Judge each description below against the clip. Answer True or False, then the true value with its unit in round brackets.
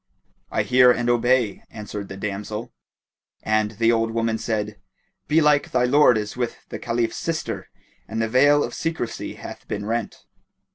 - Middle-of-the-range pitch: False (115 Hz)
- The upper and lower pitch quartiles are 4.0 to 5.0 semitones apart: False (2.8 semitones)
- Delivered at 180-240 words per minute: False (160 wpm)